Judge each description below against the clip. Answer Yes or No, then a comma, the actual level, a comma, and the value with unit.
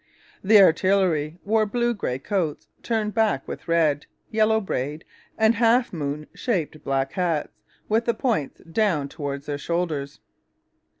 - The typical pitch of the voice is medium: Yes, medium, 175 Hz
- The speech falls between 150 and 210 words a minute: No, slow, 135 wpm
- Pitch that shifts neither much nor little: No, wide, 6.9 semitones